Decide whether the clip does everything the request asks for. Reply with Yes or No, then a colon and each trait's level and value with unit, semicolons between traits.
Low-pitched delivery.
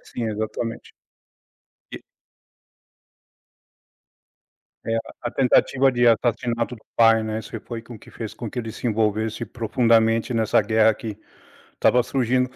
Yes: low, 115 Hz